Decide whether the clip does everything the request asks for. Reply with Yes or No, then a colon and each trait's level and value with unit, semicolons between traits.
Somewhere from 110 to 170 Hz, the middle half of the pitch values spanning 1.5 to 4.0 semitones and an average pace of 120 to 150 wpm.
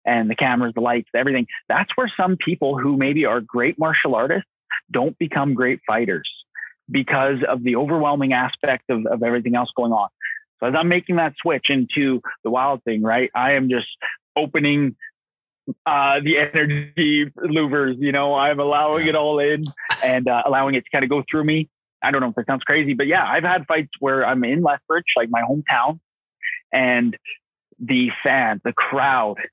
No: medium, 140 Hz; average, 3.4 semitones; average, 185 wpm